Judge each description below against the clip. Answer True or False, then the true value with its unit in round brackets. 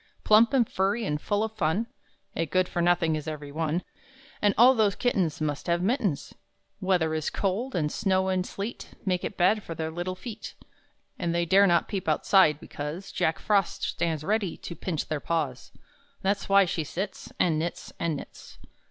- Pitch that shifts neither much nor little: True (3.9 semitones)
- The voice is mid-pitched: True (180 Hz)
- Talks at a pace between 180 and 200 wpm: True (185 wpm)